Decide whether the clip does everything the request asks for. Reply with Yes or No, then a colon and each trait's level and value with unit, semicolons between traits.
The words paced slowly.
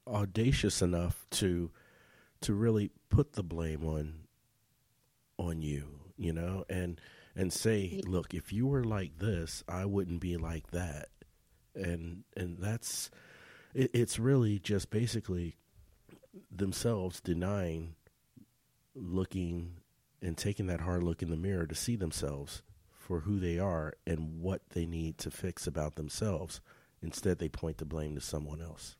No: average, 145 wpm